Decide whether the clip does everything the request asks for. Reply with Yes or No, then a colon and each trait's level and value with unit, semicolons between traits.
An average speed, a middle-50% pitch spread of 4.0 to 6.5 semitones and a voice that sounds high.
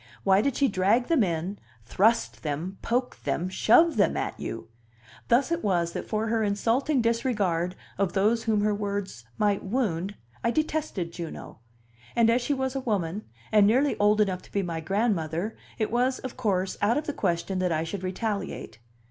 Yes: average, 180 wpm; average, 4.4 semitones; high, 205 Hz